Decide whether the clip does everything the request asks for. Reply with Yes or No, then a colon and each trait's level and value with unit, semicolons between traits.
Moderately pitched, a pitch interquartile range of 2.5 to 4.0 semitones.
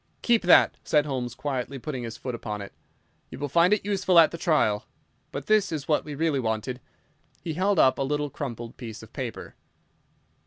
No: medium, 145 Hz; wide, 5.4 semitones